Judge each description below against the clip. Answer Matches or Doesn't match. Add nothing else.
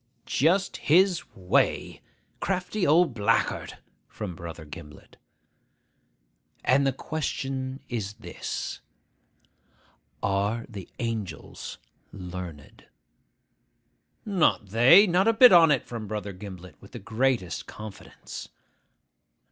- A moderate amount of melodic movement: Doesn't match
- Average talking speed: Doesn't match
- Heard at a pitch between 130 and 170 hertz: Doesn't match